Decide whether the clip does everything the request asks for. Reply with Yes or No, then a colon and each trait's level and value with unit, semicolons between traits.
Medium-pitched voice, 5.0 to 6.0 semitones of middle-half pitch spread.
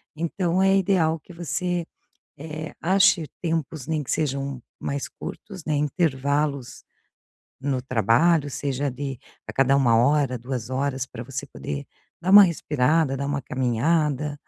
No: medium, 145 Hz; average, 3.8 semitones